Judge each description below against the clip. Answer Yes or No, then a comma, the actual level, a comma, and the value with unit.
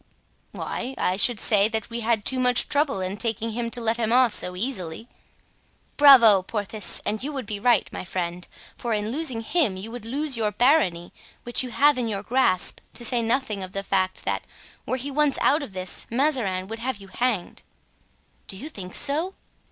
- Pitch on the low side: No, high, 230 Hz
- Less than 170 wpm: No, average, 200 wpm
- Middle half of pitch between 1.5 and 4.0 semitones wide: No, average, 4.6 semitones